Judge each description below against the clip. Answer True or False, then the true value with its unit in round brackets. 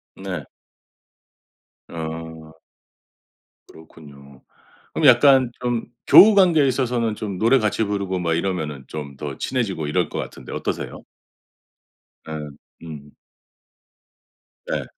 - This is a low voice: True (90 Hz)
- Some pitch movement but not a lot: False (7.4 semitones)